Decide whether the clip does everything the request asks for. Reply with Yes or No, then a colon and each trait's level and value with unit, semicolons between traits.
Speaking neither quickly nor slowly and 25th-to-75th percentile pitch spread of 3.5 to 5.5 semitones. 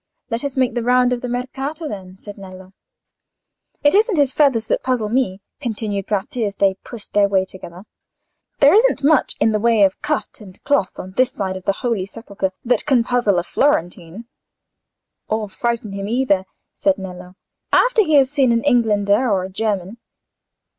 Yes: average, 180 wpm; average, 4.8 semitones